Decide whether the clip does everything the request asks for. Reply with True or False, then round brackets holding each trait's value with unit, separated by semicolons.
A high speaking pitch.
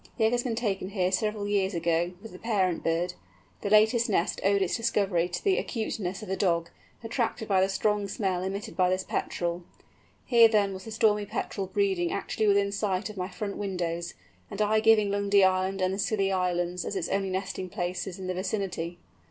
True (195 Hz)